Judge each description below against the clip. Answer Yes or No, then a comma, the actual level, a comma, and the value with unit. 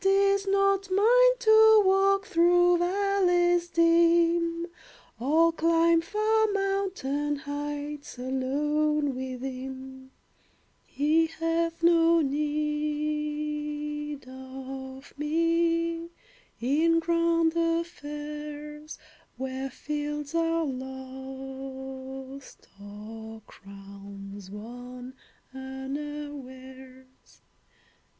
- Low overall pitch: No, very high, 300 Hz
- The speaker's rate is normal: No, slow, 70 wpm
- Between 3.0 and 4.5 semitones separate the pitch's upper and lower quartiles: Yes, average, 4.1 semitones